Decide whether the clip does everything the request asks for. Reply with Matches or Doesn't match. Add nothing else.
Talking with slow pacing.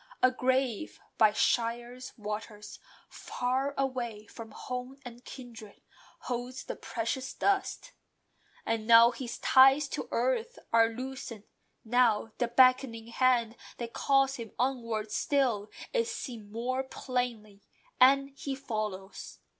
Matches